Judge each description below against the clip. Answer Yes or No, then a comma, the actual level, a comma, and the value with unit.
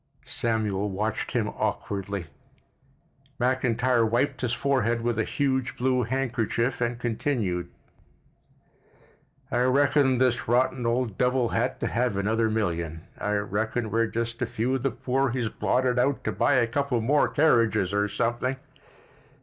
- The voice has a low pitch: Yes, low, 120 Hz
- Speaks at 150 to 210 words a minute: No, average, 140 wpm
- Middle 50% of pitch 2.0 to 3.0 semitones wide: Yes, average, 2.7 semitones